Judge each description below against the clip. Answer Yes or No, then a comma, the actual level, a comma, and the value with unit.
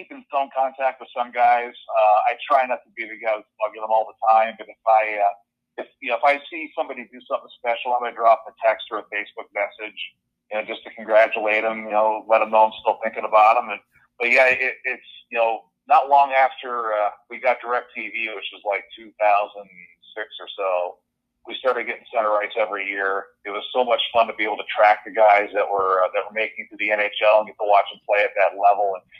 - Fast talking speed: Yes, fast, 245 wpm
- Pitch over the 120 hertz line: No, low, 110 Hz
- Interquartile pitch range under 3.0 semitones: Yes, narrow, 2.4 semitones